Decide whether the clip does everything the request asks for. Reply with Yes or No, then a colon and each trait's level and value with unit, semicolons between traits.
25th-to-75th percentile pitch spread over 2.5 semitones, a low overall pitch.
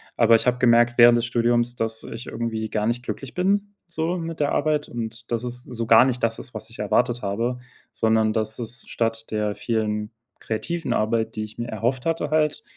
No: narrow, 2.0 semitones; low, 120 Hz